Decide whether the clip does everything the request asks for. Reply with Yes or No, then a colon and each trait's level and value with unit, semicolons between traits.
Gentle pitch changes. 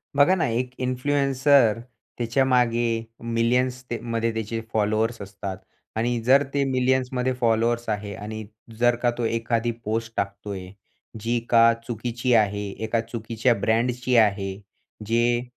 Yes: narrow, 2.1 semitones